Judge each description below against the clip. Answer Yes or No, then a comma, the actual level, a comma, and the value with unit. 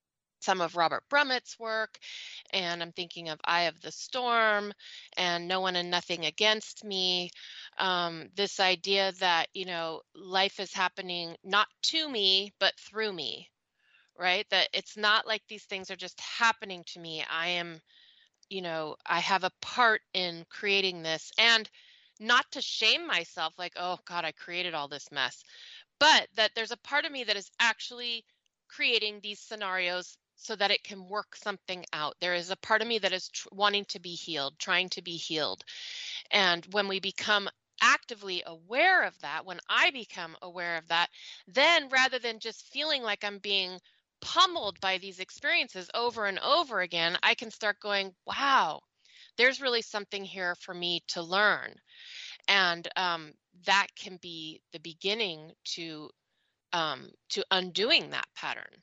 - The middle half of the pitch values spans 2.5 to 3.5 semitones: No, average, 4.0 semitones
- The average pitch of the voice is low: No, high, 195 Hz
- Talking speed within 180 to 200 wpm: No, average, 165 wpm